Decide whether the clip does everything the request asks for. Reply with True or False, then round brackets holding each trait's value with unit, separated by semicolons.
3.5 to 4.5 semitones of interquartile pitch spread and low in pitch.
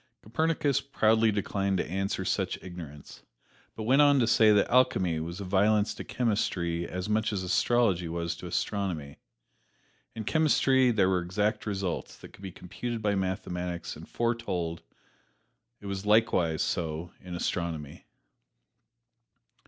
True (4.1 semitones; 100 Hz)